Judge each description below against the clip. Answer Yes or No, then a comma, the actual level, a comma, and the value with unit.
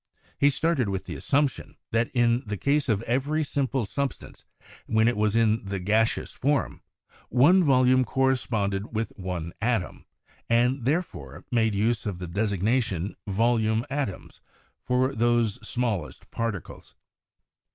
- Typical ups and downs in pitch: Yes, average, 3.9 semitones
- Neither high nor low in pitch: No, low, 115 Hz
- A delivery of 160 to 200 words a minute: No, slow, 135 wpm